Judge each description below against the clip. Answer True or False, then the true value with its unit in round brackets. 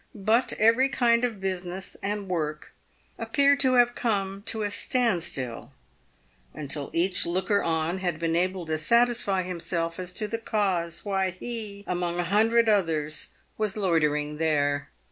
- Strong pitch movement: False (4.7 semitones)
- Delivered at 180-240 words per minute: False (155 wpm)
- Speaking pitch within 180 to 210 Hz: True (190 Hz)